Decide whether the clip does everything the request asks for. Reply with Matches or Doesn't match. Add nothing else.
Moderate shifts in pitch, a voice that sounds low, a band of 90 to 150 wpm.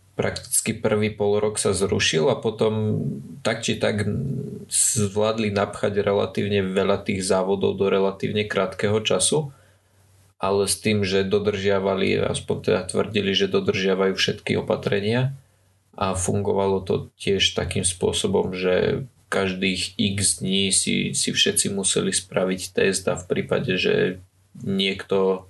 Doesn't match